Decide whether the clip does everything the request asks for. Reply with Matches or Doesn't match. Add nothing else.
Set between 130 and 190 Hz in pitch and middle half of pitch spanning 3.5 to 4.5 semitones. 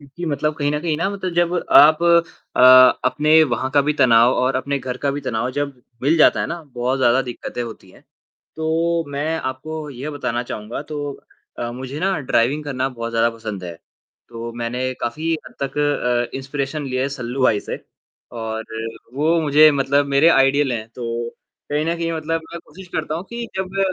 Matches